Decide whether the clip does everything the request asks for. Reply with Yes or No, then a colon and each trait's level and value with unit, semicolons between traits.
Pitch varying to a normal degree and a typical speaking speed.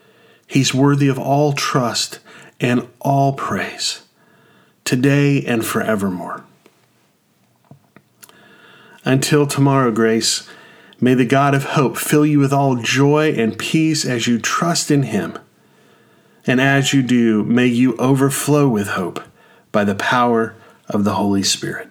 No: average, 3.3 semitones; slow, 130 wpm